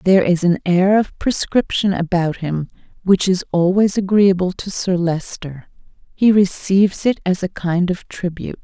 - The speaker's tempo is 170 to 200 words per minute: No, average, 160 wpm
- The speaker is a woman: Yes, female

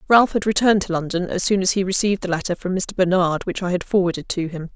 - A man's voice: No, female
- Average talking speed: No, fast, 265 wpm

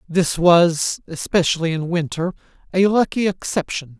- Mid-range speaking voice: Yes, medium, 175 Hz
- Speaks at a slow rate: Yes, slow, 120 wpm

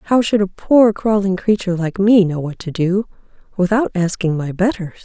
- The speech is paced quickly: No, average, 190 wpm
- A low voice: No, high, 195 Hz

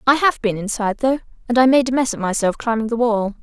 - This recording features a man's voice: No, female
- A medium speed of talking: No, fast, 265 wpm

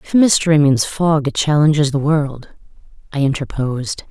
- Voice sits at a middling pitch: Yes, medium, 145 Hz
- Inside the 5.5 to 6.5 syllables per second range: No, 5.0 syllables/s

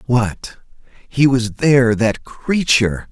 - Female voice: No, male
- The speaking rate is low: Yes, slow, 115 wpm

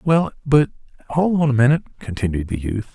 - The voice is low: Yes, low, 130 Hz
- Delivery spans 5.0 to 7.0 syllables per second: Yes, 5.2 syllables/s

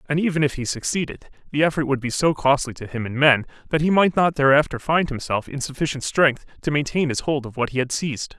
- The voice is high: No, medium, 140 Hz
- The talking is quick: Yes, fast, 245 wpm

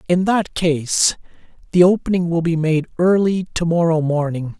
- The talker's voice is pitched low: No, medium, 170 Hz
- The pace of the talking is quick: No, average, 145 wpm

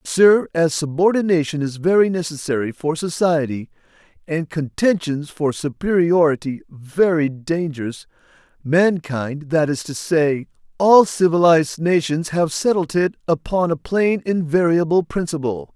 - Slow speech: Yes, slow, 120 wpm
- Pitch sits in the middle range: Yes, medium, 160 Hz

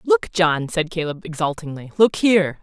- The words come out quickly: No, average, 160 wpm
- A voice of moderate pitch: Yes, medium, 160 Hz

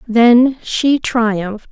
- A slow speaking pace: Yes, slow, 105 wpm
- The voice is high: Yes, high, 235 Hz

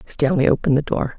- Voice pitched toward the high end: No, medium, 145 Hz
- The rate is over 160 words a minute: Yes, fast, 205 wpm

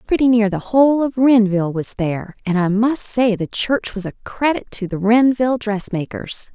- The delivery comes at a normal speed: Yes, average, 190 wpm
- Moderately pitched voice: No, high, 220 Hz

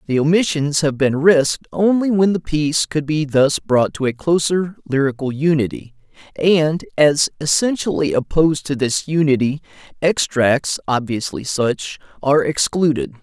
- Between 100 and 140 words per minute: Yes, slow, 135 wpm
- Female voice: No, male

